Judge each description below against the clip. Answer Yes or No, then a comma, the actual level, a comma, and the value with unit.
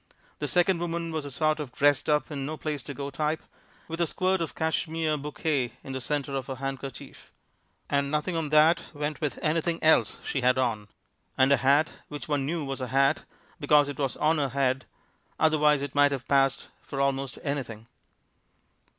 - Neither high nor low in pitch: Yes, medium, 145 Hz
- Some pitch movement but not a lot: No, narrow, 2.3 semitones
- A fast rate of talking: No, average, 195 wpm